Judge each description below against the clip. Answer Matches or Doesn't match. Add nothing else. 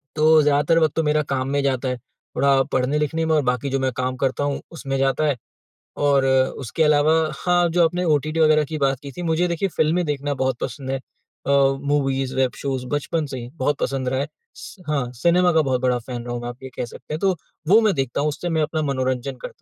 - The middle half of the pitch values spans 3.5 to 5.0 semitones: Doesn't match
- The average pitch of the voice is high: Doesn't match